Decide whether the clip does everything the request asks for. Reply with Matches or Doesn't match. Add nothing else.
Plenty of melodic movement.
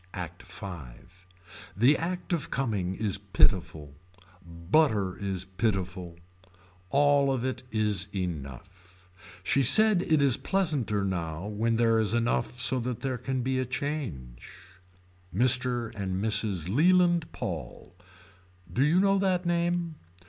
Matches